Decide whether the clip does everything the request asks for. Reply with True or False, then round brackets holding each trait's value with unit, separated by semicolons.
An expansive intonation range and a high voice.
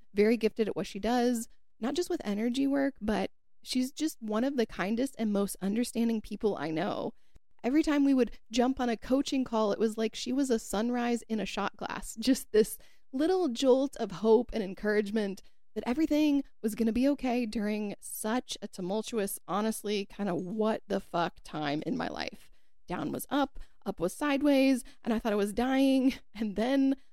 False (3.9 semitones; 225 Hz)